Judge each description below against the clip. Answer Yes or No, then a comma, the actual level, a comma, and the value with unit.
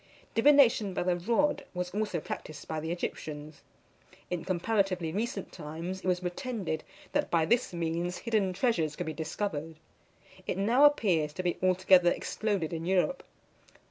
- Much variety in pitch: No, average, 4.5 semitones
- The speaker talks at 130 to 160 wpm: Yes, average, 150 wpm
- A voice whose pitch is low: No, medium, 180 Hz